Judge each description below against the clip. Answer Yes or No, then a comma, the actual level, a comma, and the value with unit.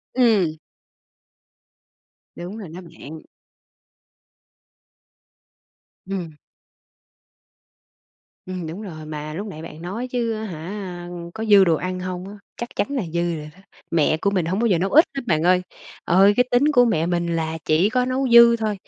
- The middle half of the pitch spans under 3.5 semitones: No, average, 4.9 semitones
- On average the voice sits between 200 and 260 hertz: No, medium, 185 Hz